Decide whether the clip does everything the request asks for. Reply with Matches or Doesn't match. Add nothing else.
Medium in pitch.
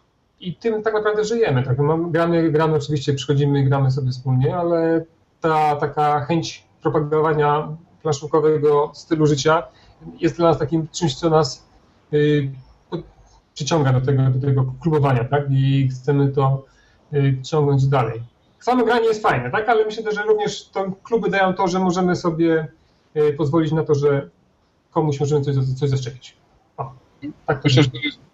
Matches